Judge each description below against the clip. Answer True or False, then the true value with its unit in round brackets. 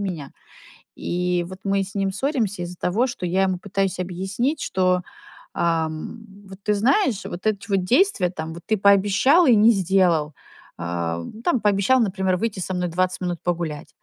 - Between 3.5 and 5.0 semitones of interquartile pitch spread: False (2.8 semitones)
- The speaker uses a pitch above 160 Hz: True (190 Hz)